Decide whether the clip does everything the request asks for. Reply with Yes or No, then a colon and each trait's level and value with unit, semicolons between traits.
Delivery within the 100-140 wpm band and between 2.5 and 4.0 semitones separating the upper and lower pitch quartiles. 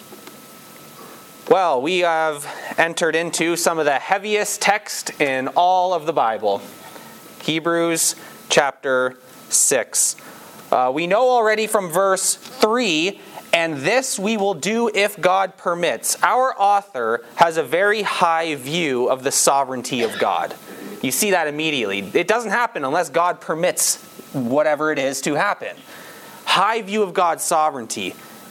No: slow, 135 wpm; average, 4.9 semitones